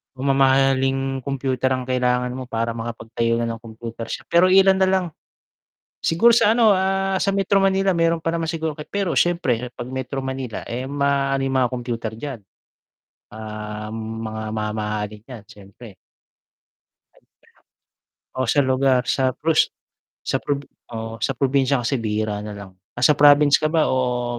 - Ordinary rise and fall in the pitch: Yes, average, 4.2 semitones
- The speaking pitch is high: No, low, 130 Hz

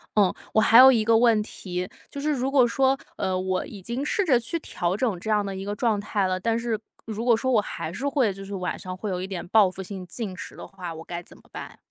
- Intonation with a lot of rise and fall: No, average, 4.2 semitones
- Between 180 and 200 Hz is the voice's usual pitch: No, high, 210 Hz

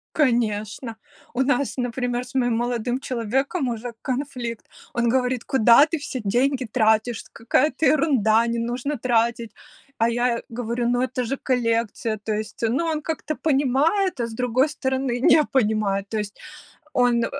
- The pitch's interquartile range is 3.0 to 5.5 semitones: No, narrow, 2.5 semitones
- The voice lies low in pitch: No, high, 245 Hz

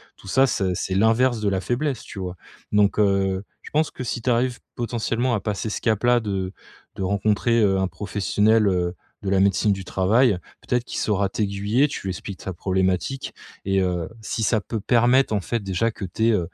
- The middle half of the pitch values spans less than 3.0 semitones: No, average, 3.5 semitones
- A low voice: Yes, low, 105 Hz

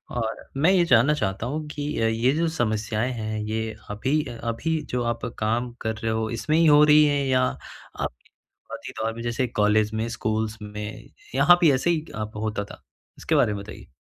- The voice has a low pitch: Yes, low, 115 Hz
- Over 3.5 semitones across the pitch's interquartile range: Yes, average, 5.0 semitones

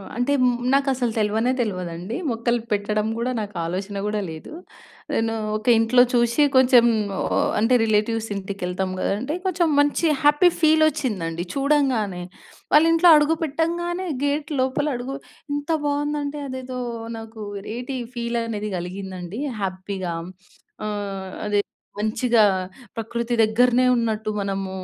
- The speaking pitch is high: Yes, high, 230 Hz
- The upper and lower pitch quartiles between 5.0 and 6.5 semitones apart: Yes, average, 5.3 semitones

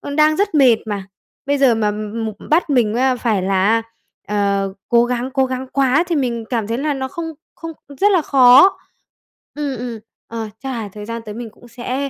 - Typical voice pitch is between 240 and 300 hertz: Yes, high, 245 Hz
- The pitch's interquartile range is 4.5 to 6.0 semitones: No, average, 3.8 semitones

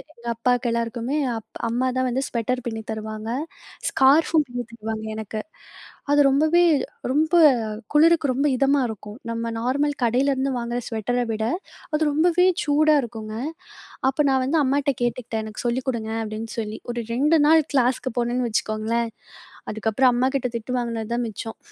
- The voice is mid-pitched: No, high, 245 Hz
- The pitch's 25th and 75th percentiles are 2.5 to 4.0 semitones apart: Yes, average, 3.4 semitones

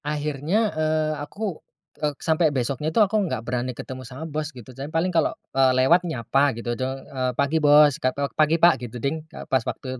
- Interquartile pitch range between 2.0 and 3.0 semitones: No, average, 3.5 semitones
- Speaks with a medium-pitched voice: Yes, medium, 145 Hz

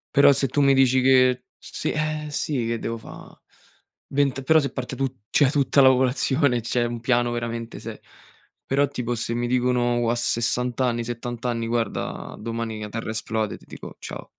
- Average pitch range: No, narrow, 2.3 semitones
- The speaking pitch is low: Yes, low, 125 Hz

